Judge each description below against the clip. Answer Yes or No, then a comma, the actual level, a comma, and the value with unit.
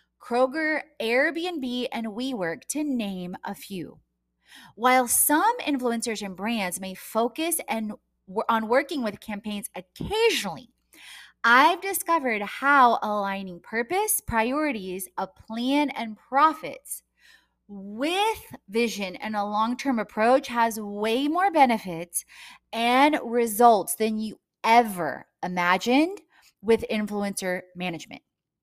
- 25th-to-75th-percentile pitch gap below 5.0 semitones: No, average, 5.3 semitones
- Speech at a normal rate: No, slow, 105 wpm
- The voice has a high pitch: Yes, high, 230 Hz